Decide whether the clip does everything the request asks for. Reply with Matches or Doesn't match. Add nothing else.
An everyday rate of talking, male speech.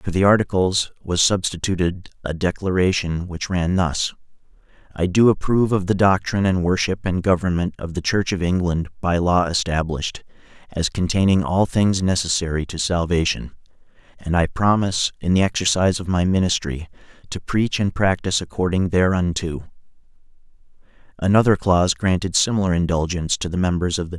Matches